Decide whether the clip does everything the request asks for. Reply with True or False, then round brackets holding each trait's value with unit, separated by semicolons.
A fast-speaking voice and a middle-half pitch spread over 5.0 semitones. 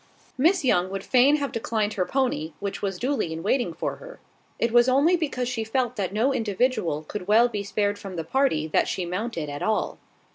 True (210 wpm; 5.6 semitones)